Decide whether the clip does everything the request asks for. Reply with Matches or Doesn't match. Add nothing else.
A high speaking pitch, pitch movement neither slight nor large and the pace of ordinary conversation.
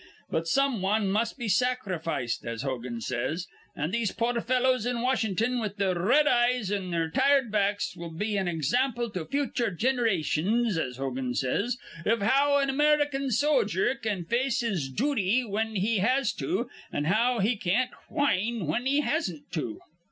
Doesn't match